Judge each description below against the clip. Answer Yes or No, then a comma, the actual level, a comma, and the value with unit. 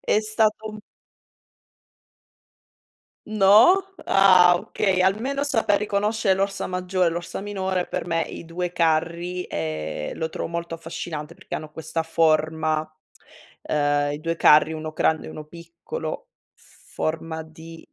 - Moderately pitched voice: Yes, medium, 170 Hz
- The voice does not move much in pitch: No, average, 3.7 semitones